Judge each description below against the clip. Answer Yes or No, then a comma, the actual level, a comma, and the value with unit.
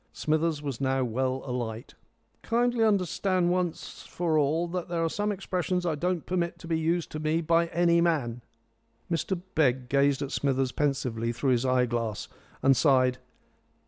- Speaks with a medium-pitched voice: Yes, medium, 155 Hz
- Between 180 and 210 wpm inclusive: No, average, 165 wpm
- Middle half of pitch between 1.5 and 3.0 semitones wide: No, average, 4.9 semitones